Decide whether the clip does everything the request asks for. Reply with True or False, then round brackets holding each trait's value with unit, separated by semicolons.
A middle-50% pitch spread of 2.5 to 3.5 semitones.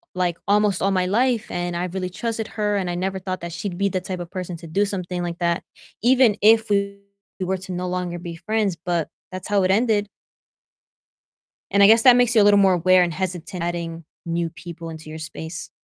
True (2.8 semitones)